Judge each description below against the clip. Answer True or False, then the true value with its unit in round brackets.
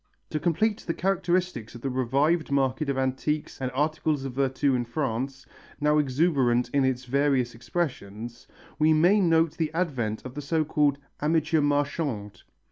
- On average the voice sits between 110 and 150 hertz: True (140 Hz)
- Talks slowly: False (155 wpm)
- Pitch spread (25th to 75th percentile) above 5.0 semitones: False (3.6 semitones)